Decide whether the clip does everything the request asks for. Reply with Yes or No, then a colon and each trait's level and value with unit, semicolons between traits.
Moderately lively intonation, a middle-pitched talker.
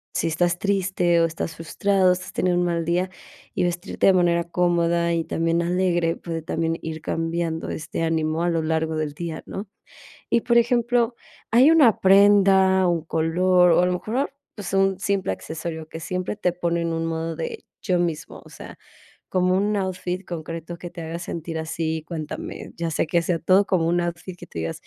No: narrow, 2.3 semitones; medium, 175 Hz